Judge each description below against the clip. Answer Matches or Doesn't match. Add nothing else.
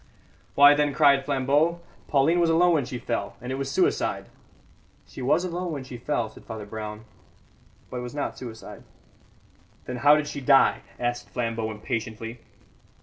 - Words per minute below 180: Matches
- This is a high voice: Doesn't match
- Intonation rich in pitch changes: Doesn't match